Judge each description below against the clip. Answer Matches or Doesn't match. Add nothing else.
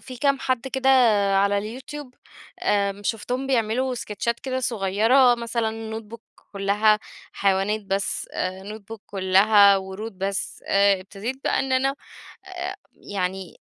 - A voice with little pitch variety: Doesn't match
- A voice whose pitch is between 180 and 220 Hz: Matches